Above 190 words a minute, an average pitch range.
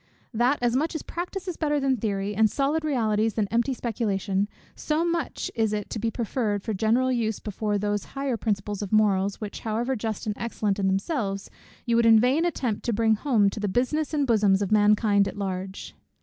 Yes: fast, 205 wpm; average, 3.9 semitones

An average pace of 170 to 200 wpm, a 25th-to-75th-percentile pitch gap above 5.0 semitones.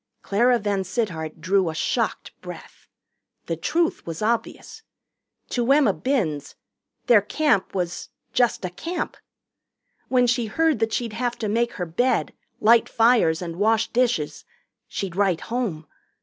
No: slow, 135 wpm; wide, 5.4 semitones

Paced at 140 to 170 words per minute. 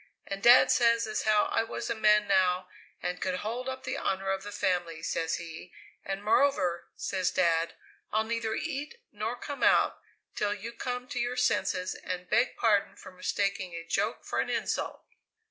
No: average, 180 wpm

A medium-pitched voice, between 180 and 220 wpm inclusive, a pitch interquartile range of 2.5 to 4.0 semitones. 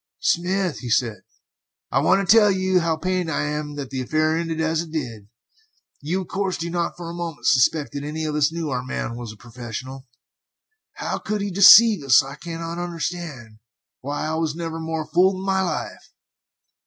Yes: medium, 160 Hz; average, 195 wpm; average, 3.7 semitones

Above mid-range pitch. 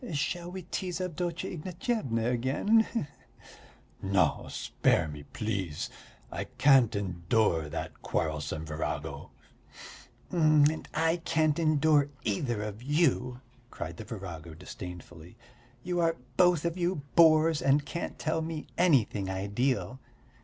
No: medium, 140 Hz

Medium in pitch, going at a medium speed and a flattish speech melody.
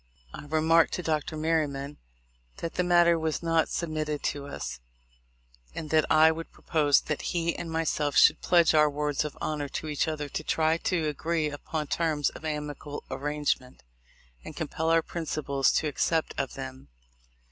Yes: medium, 155 Hz; average, 165 wpm; narrow, 1.9 semitones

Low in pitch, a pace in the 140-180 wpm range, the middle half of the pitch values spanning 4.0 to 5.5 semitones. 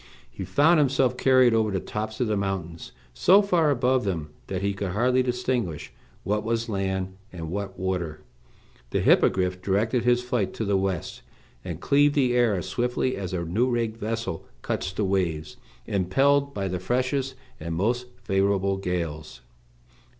Yes: low, 100 Hz; average, 165 wpm; average, 5.0 semitones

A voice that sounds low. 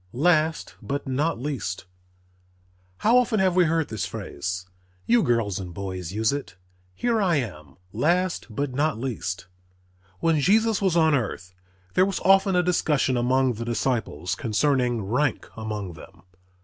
Yes: low, 130 Hz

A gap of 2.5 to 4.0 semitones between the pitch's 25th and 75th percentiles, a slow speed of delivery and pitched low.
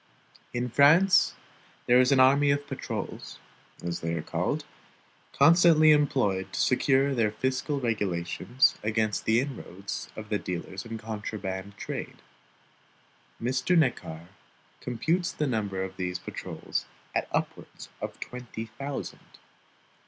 No: wide, 5.6 semitones; slow, 125 wpm; low, 120 Hz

